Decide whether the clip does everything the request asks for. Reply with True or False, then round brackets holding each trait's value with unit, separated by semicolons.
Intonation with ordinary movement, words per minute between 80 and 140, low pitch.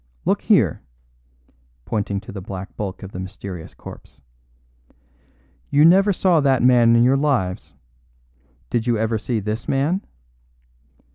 False (5.7 semitones; 135 wpm; 115 Hz)